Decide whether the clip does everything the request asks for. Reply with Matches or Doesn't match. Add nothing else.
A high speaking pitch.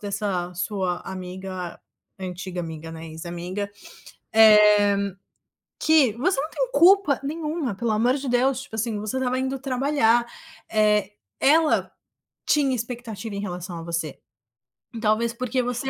Matches